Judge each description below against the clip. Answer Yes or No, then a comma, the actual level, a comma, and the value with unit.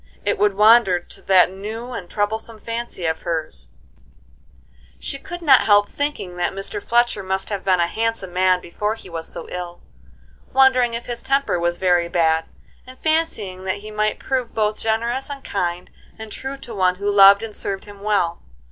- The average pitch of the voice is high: Yes, high, 205 Hz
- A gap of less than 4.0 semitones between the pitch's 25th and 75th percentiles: No, average, 4.3 semitones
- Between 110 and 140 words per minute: No, average, 185 wpm